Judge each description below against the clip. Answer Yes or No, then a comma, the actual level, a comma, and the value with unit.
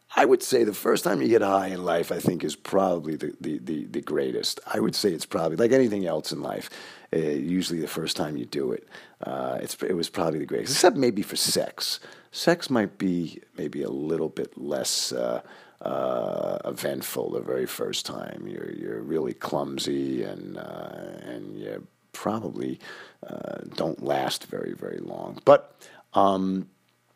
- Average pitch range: Yes, average, 3.8 semitones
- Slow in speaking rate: No, average, 180 wpm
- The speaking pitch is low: Yes, very low, 95 Hz